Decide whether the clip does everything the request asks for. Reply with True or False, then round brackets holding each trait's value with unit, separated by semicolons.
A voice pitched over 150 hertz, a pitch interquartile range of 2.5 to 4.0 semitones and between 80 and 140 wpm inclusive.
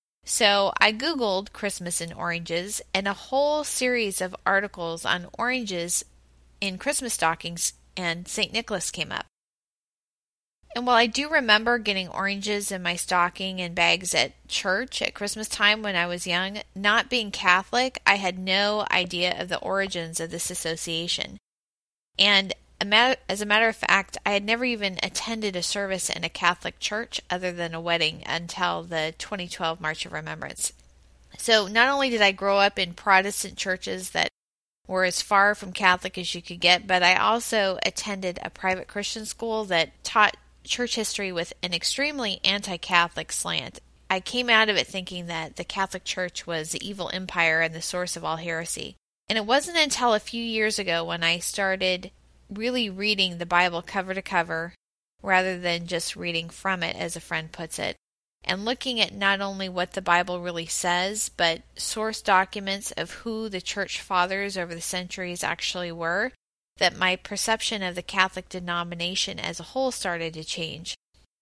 False (185 Hz; 3.3 semitones; 175 wpm)